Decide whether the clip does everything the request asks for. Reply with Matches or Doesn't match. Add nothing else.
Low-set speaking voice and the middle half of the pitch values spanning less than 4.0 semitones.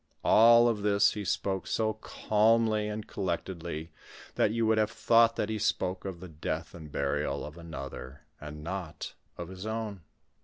Doesn't match